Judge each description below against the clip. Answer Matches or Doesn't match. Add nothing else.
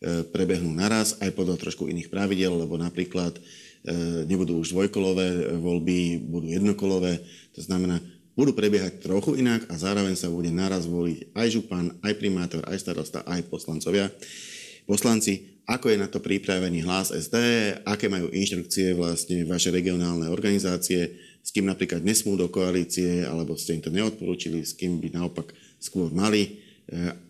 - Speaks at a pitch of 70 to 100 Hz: Matches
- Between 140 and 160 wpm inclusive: Matches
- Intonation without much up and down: Matches